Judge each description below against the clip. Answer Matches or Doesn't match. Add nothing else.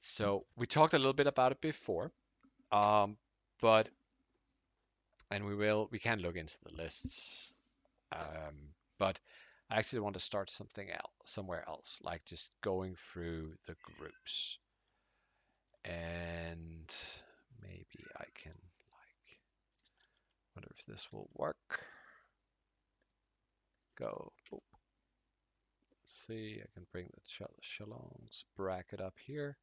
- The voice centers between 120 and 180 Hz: Doesn't match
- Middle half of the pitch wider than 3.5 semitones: Matches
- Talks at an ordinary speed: Doesn't match